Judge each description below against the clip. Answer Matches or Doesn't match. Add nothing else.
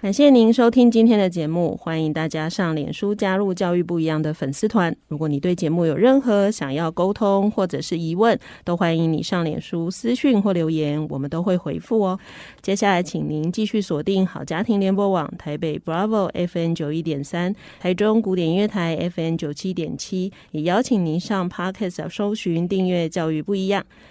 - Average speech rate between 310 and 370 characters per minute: Matches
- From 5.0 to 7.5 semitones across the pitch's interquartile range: Doesn't match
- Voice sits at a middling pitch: Matches